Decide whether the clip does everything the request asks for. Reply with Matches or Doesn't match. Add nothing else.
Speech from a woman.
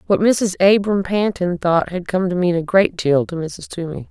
Matches